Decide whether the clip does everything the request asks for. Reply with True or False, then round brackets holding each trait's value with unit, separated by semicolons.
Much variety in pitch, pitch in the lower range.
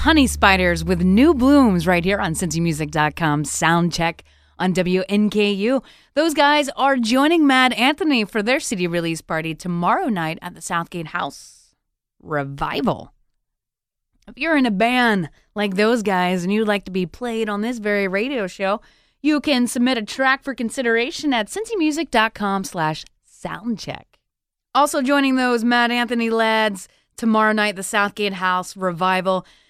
False (5.7 semitones; 210 Hz)